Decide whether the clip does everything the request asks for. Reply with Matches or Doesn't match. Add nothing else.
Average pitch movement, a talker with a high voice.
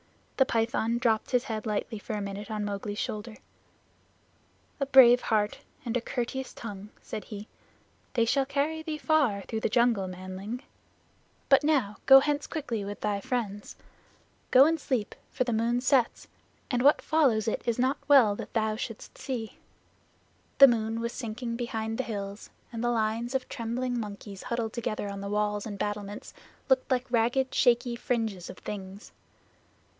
Matches